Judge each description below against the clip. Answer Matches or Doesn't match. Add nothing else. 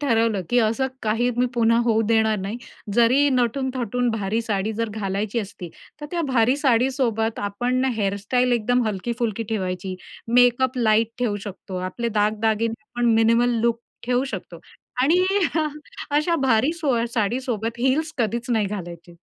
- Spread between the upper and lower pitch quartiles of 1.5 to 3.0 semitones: Matches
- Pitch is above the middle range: Matches